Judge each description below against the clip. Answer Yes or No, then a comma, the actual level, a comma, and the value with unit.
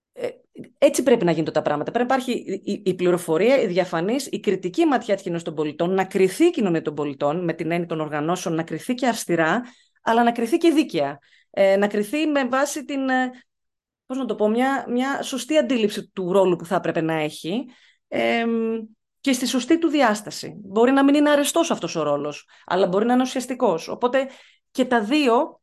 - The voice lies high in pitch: Yes, high, 225 Hz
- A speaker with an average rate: No, fast, 195 wpm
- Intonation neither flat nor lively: No, wide, 7.3 semitones